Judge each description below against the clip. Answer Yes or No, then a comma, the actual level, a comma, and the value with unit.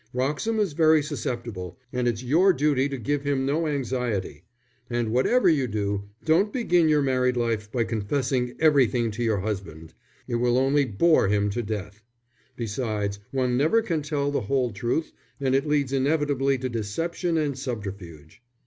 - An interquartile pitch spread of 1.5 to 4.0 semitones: No, average, 5.1 semitones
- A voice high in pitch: No, low, 130 Hz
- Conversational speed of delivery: Yes, average, 165 wpm